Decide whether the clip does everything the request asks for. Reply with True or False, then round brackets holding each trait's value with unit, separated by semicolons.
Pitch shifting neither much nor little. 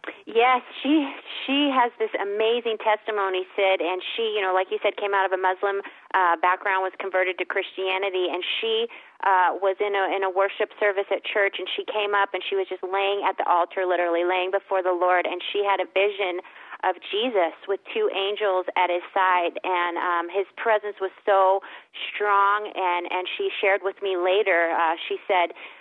False (2.1 semitones)